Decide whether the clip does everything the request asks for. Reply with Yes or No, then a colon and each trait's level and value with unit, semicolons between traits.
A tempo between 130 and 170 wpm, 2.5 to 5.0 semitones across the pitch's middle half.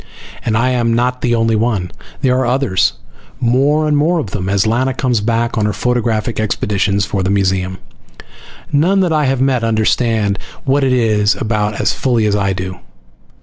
No: average, 185 wpm; average, 3.7 semitones